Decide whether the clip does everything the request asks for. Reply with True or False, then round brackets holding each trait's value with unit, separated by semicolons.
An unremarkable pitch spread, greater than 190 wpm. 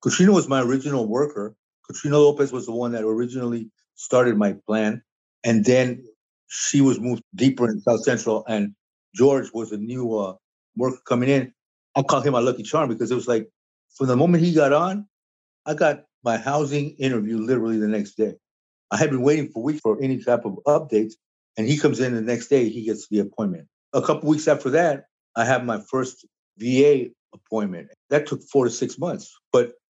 True (4.4 semitones; 200 wpm)